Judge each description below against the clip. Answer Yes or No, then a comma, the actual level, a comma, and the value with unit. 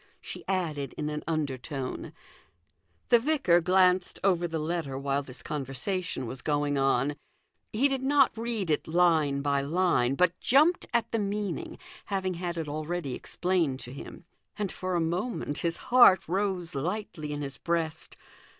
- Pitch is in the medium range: Yes, medium, 170 Hz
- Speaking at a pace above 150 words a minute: Yes, average, 160 wpm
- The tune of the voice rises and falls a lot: No, average, 4.7 semitones